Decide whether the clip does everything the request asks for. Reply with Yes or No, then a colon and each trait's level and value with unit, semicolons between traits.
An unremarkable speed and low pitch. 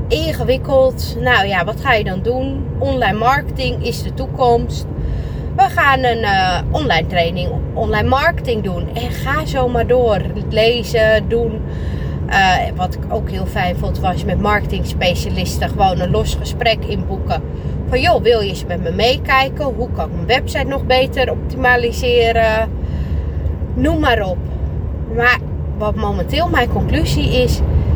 Yes: average, 150 wpm; very low, 90 Hz